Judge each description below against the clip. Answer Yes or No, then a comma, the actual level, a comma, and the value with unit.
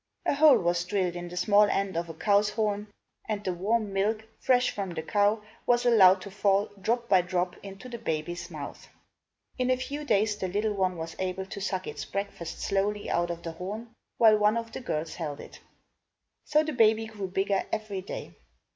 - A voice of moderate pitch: No, high, 200 Hz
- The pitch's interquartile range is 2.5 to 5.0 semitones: Yes, average, 3.2 semitones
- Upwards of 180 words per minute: Yes, average, 200 wpm